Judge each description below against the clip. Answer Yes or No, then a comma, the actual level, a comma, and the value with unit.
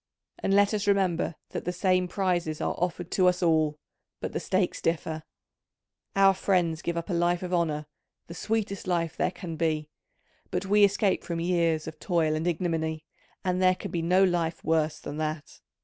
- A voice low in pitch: No, medium, 175 Hz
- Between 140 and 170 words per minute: No, average, 185 wpm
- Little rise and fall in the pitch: Yes, narrow, 2.3 semitones